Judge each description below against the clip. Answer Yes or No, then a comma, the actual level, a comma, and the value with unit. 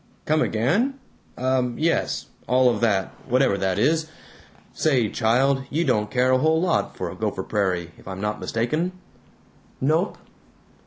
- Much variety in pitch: Yes, wide, 6.4 semitones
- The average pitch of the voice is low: Yes, low, 130 Hz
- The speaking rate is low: No, average, 145 wpm